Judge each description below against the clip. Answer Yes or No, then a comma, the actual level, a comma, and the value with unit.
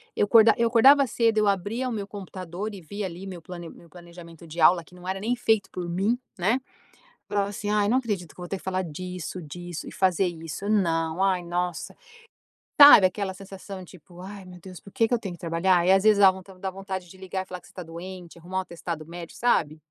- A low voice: No, medium, 185 Hz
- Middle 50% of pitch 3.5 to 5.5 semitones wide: No, average, 2.7 semitones